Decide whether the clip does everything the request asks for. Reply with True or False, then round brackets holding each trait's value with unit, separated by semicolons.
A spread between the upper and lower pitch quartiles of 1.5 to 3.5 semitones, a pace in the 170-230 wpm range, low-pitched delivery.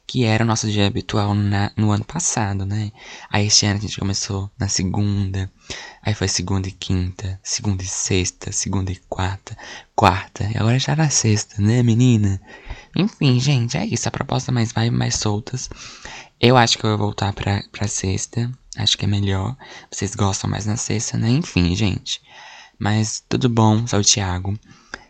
True (3.1 semitones; 180 wpm; 105 Hz)